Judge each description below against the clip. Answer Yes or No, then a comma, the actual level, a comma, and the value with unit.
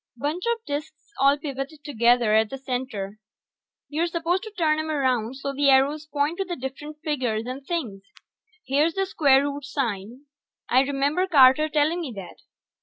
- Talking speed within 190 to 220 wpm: No, average, 170 wpm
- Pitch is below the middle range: No, very high, 280 Hz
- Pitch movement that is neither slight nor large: Yes, average, 3.2 semitones